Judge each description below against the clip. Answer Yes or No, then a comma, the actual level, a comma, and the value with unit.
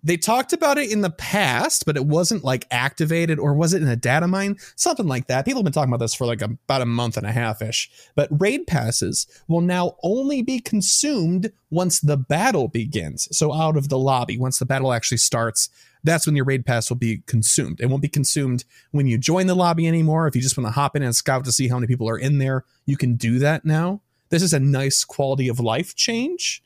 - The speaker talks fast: Yes, fast, 245 wpm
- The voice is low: No, medium, 145 Hz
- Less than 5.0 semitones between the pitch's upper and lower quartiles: No, wide, 5.6 semitones